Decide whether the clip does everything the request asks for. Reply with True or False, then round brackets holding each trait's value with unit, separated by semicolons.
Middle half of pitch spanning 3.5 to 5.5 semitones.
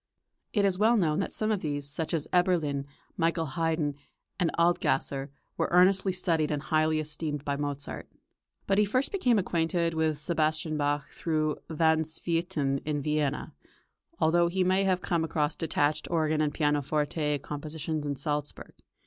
False (2.8 semitones)